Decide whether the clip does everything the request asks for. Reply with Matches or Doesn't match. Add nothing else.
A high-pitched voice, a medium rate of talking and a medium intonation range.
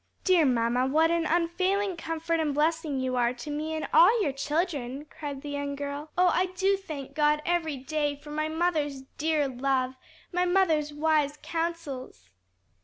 Matches